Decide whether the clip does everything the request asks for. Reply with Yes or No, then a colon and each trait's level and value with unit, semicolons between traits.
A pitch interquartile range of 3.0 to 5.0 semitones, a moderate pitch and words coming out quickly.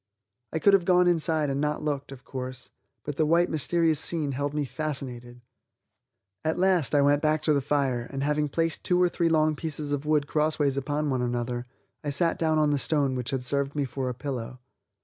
No: narrow, 2.5 semitones; medium, 145 Hz; fast, 210 wpm